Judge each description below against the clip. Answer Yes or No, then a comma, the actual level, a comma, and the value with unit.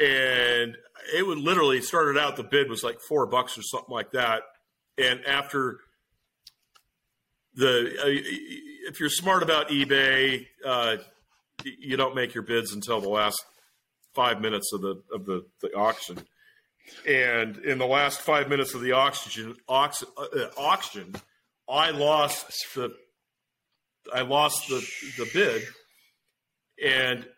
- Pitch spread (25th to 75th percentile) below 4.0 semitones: Yes, average, 2.8 semitones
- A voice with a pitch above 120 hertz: Yes, low, 130 Hz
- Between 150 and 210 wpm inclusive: No, average, 140 wpm